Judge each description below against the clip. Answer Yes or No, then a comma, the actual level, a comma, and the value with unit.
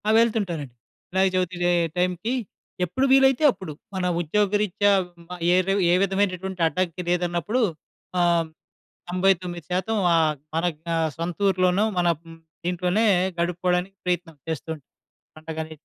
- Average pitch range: No, narrow, 2.3 semitones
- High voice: No, medium, 180 Hz